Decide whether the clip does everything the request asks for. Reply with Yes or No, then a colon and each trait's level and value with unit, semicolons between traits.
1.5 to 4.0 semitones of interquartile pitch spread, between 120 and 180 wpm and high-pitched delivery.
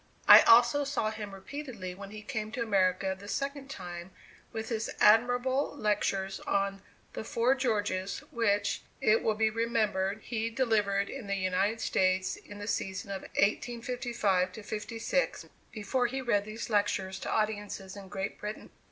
Yes: average, 3.0 semitones; average, 150 wpm; high, 215 Hz